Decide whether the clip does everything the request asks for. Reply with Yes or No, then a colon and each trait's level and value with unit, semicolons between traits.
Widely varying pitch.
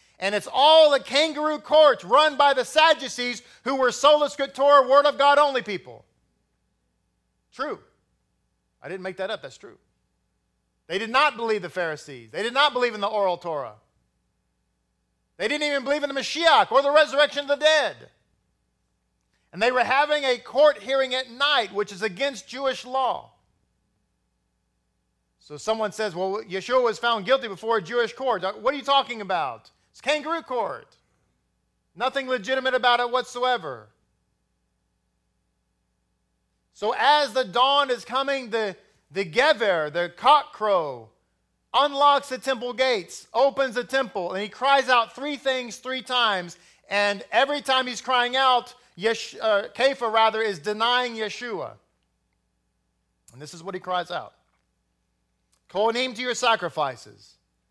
Yes: wide, 7.5 semitones